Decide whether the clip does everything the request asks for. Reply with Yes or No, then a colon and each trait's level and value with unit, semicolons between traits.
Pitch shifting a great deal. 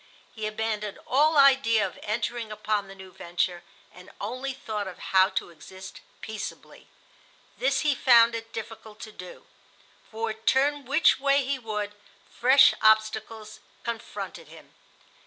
No: average, 3.7 semitones